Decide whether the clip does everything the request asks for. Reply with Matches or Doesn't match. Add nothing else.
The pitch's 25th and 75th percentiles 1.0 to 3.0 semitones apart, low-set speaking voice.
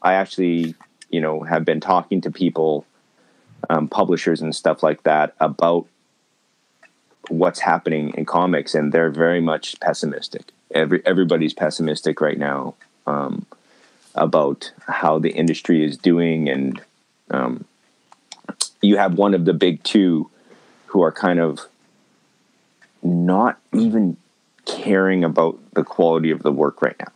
Matches